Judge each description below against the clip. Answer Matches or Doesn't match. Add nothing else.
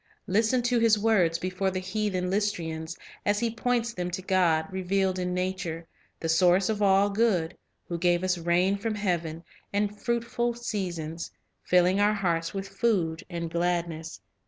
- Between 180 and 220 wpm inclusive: Doesn't match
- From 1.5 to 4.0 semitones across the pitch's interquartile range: Matches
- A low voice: Doesn't match